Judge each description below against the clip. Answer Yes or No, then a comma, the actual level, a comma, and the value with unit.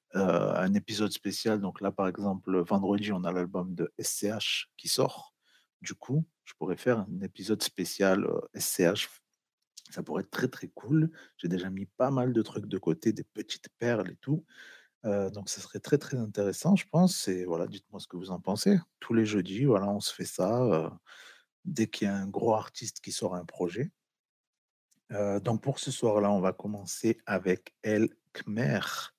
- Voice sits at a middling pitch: No, low, 100 Hz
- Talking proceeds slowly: No, average, 195 wpm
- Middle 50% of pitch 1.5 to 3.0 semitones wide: No, average, 3.7 semitones